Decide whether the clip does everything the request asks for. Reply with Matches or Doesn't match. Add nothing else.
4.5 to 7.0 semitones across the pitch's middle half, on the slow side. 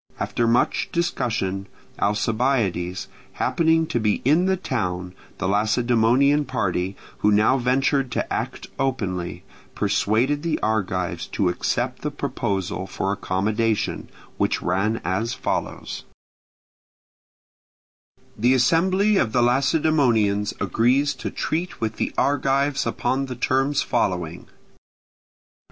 Matches